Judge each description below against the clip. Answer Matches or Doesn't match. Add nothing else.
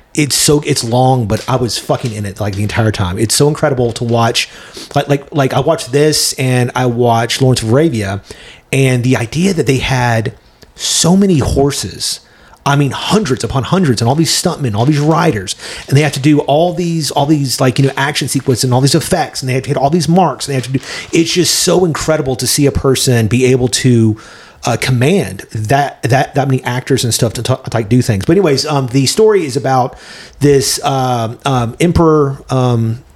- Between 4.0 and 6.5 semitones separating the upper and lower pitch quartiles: Doesn't match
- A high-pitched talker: Doesn't match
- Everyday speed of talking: Doesn't match